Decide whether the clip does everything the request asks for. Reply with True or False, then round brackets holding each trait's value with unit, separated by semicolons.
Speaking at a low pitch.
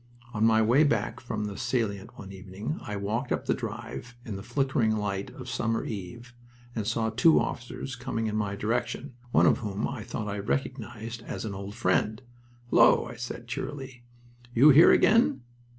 True (115 Hz)